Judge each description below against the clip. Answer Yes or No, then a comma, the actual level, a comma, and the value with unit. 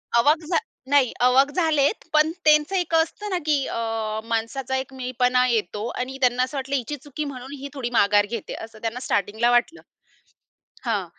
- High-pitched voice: Yes, very high, 255 Hz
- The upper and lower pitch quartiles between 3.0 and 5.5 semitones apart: Yes, average, 4.0 semitones